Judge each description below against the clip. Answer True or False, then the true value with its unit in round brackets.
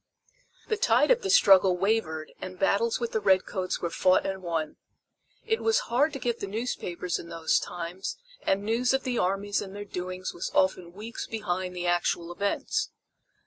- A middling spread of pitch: True (4.3 semitones)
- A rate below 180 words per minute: False (185 wpm)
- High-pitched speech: True (195 Hz)